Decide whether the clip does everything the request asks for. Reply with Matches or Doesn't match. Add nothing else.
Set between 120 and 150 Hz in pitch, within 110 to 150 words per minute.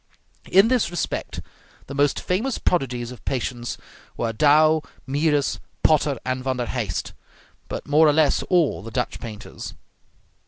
Matches